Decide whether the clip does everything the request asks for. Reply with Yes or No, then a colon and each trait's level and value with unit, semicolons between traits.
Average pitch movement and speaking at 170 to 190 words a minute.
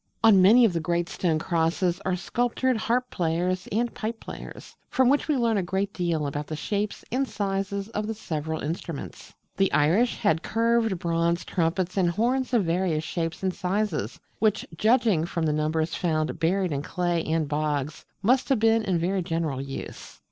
Yes: average, 5.0 semitones; average, 180 wpm